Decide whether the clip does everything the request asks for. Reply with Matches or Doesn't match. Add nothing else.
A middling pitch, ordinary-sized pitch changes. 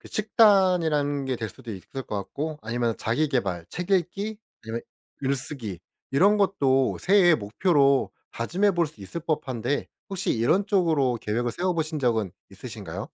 Doesn't match